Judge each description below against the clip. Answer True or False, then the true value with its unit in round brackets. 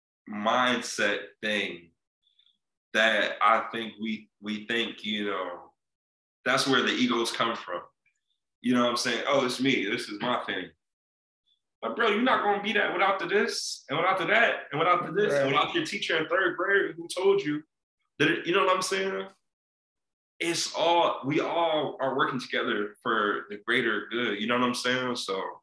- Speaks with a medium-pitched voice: False (125 Hz)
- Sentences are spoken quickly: False (190 wpm)